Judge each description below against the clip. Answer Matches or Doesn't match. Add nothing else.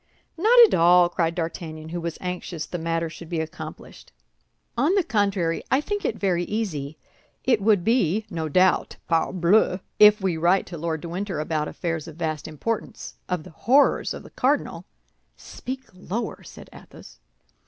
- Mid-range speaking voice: Matches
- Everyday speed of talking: Matches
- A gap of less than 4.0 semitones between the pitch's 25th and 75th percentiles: Doesn't match